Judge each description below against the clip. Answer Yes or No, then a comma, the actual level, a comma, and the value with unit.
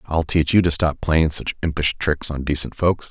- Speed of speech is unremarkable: No, fast, 230 wpm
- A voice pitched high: No, very low, 80 Hz